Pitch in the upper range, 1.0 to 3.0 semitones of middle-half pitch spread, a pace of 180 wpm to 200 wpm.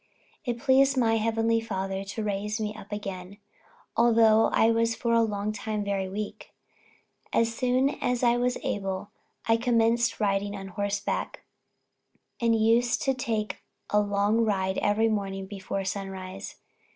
No: high, 215 Hz; narrow, 2.5 semitones; average, 145 wpm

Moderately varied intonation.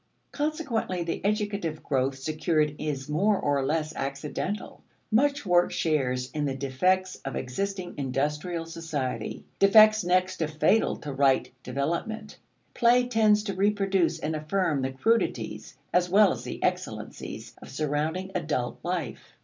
No: wide, 5.9 semitones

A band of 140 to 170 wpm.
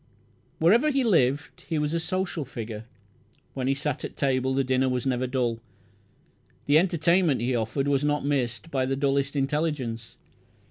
Yes: average, 160 wpm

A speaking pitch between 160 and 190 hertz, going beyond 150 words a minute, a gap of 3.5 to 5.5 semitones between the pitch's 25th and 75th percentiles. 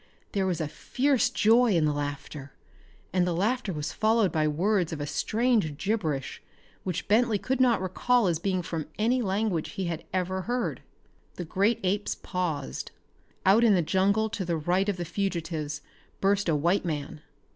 Yes: medium, 185 Hz; average, 170 wpm; average, 4.9 semitones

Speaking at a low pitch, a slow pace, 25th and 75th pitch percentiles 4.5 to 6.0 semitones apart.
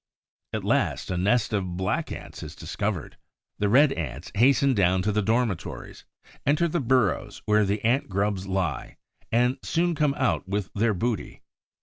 No: low, 105 Hz; average, 160 wpm; average, 5.1 semitones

